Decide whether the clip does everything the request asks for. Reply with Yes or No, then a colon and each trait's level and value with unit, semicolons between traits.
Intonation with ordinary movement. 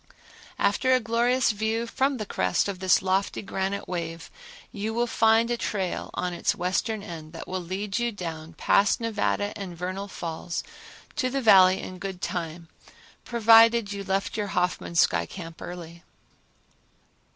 Yes: average, 4.0 semitones